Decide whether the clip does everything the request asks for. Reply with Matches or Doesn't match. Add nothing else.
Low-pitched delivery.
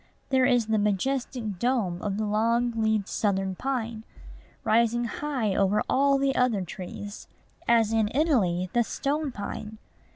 Doesn't match